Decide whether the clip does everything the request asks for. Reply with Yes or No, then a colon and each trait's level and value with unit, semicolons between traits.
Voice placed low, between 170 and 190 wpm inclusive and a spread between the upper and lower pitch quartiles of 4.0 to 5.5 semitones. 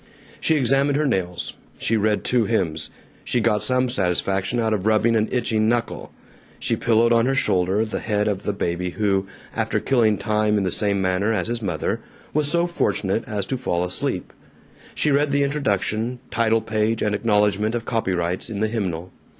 No: low, 110 Hz; average, 185 wpm; average, 3.4 semitones